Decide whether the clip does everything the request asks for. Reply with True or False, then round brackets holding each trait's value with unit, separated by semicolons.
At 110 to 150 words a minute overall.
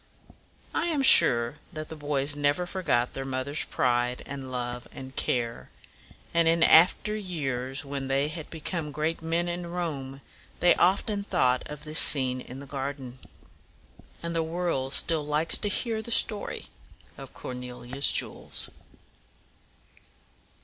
True (140 wpm)